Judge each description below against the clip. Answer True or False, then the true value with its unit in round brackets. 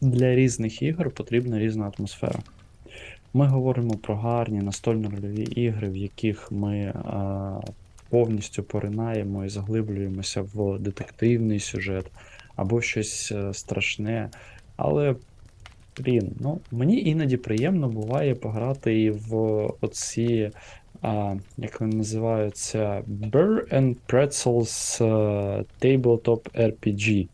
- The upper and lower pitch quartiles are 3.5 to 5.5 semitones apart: False (2.6 semitones)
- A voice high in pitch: False (110 Hz)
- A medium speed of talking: False (100 wpm)